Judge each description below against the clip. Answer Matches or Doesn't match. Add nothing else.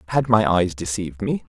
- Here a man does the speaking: Matches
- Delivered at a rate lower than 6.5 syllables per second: Matches